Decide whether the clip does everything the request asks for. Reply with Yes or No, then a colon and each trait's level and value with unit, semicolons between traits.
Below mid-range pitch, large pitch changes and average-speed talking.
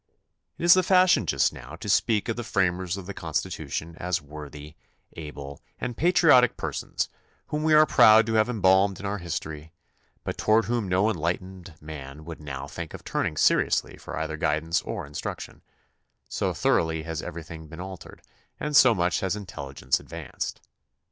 Yes: very low, 90 Hz; wide, 5.9 semitones; average, 175 wpm